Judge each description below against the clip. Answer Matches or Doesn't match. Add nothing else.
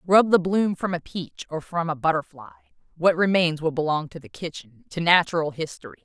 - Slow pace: Doesn't match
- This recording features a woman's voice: Matches